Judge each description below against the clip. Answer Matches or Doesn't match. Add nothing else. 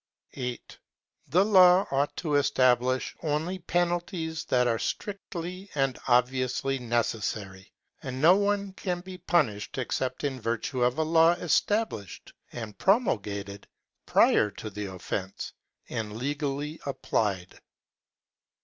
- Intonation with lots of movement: Matches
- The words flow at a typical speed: Doesn't match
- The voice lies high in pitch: Doesn't match